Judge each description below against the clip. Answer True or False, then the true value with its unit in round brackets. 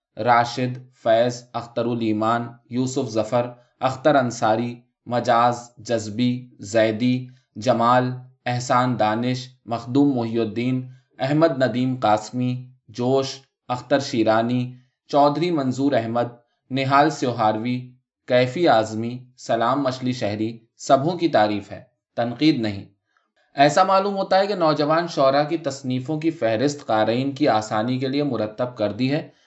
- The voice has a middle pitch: False (125 Hz)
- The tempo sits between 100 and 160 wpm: True (120 wpm)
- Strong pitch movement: False (2.7 semitones)